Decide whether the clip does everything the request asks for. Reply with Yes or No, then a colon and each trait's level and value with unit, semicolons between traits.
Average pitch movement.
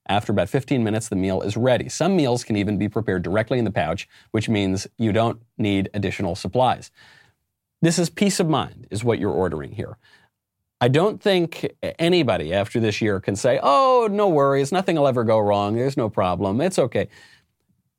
No: wide, 5.7 semitones